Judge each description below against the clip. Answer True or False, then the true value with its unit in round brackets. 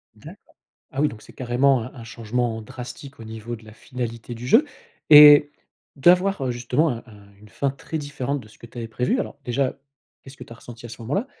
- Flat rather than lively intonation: False (3.5 semitones)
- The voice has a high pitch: False (125 Hz)